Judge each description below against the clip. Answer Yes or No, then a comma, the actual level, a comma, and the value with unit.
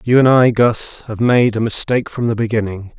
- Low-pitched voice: Yes, low, 115 Hz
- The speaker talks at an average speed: No, fast, 220 wpm